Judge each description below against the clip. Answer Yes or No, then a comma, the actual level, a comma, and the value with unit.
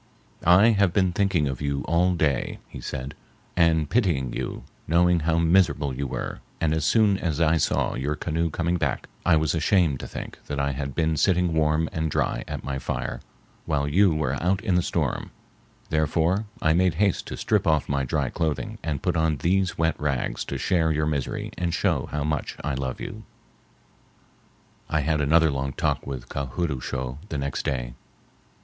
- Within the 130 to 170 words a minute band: No, average, 190 wpm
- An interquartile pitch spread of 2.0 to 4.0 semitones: Yes, average, 3.5 semitones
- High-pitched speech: No, very low, 80 Hz